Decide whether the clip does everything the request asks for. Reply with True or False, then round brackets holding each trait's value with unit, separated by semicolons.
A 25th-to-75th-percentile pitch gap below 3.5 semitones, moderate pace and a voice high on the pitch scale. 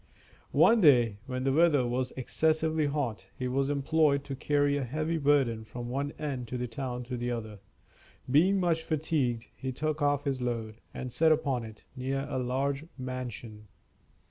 False (3.1 semitones; 170 wpm; 135 Hz)